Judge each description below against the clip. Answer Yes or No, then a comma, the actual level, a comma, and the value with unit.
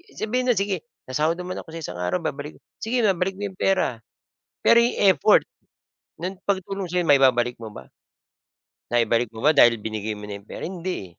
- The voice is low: No, medium, 165 Hz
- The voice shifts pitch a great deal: Yes, wide, 8.6 semitones